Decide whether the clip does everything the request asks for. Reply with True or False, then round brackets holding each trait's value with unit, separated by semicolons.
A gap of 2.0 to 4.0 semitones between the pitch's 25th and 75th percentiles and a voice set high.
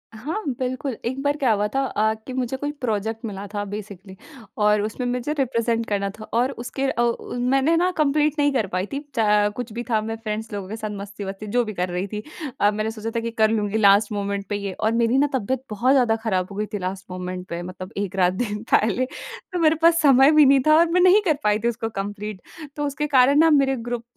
False (4.6 semitones; 220 Hz)